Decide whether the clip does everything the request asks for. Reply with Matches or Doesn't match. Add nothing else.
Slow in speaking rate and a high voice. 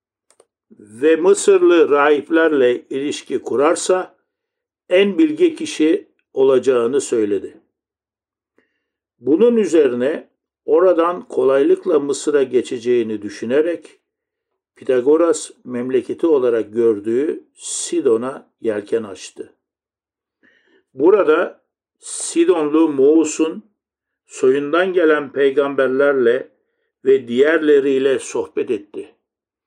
Matches